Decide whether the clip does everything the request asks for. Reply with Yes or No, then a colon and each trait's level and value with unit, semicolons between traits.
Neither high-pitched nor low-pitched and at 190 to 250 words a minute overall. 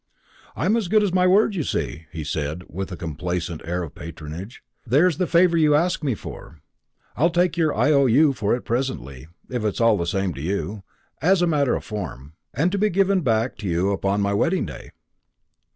No: low, 115 Hz; average, 200 wpm